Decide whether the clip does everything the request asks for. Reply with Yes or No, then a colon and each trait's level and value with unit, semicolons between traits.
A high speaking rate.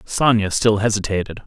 No: slow, 125 wpm